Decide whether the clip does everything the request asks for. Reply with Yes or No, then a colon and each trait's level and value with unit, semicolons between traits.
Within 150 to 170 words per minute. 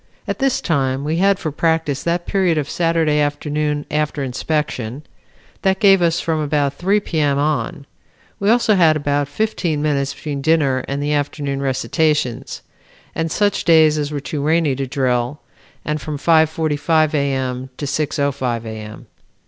Yes: average, 165 wpm